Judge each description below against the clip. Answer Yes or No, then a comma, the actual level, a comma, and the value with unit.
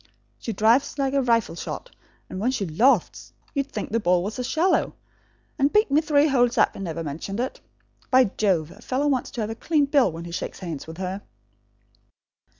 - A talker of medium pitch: No, high, 235 Hz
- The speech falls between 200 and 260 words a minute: Yes, fast, 205 wpm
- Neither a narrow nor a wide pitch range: No, wide, 6.8 semitones